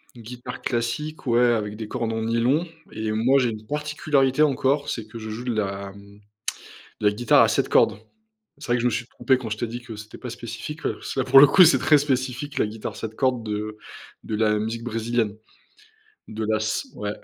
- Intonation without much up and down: No, average, 3.2 semitones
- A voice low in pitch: Yes, low, 115 Hz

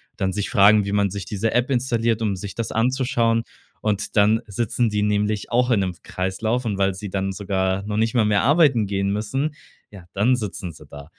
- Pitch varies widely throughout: No, average, 2.8 semitones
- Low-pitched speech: Yes, low, 105 Hz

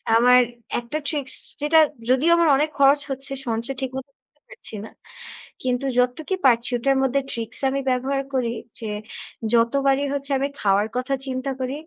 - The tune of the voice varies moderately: No, narrow, 2.0 semitones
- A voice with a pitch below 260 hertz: No, very high, 265 Hz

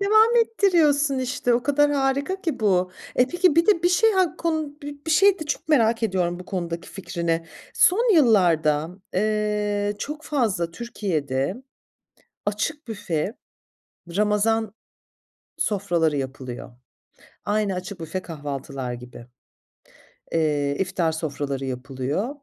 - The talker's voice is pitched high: Yes, high, 205 Hz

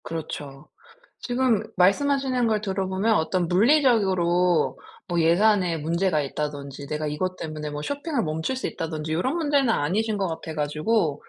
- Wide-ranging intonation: Yes, wide, 6.3 semitones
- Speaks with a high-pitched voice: No, medium, 180 Hz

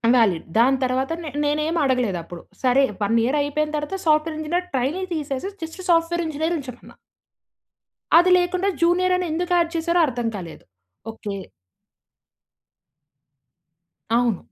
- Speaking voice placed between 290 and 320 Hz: Yes, very high, 300 Hz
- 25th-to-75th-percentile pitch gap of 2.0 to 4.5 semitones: No, average, 5.3 semitones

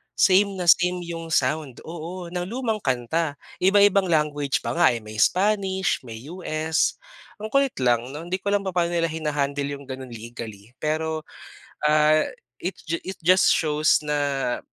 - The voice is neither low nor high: Yes, medium, 160 Hz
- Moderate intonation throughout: Yes, average, 4.6 semitones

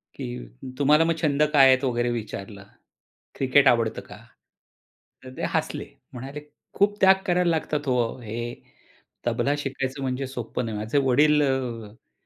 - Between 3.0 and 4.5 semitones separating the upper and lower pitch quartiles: Yes, average, 3.7 semitones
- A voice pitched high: No, low, 135 Hz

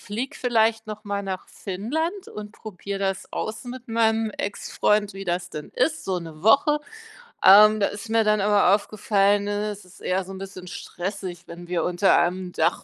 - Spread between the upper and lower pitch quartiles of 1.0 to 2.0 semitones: No, average, 2.7 semitones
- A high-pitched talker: Yes, high, 205 Hz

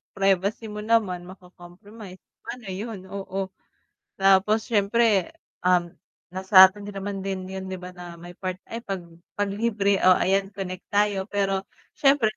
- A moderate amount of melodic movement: No, narrow, 1.8 semitones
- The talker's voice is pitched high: Yes, high, 195 Hz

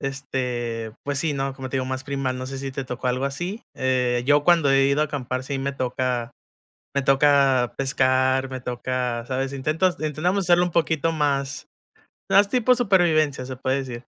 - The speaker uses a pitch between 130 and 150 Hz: Yes, low, 135 Hz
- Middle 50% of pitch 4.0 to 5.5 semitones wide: No, narrow, 2.5 semitones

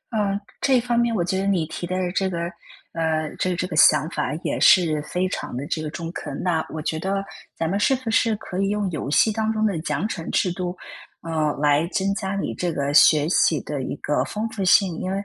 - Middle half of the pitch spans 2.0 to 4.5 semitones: Yes, average, 4.0 semitones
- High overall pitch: No, medium, 180 Hz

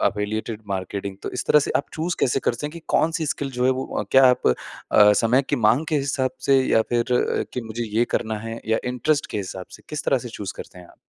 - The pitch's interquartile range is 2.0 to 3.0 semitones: No, average, 4.1 semitones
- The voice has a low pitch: Yes, low, 120 Hz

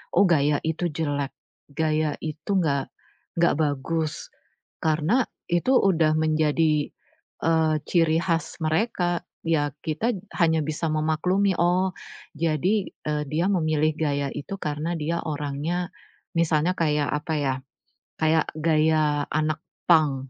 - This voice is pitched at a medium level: Yes, medium, 155 Hz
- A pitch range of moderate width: No, narrow, 2.1 semitones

